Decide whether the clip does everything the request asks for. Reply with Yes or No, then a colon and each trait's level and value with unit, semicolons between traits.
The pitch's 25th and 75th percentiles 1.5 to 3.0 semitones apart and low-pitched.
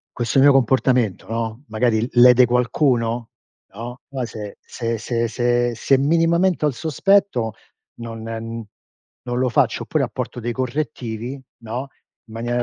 Yes: narrow, 2.5 semitones; low, 120 Hz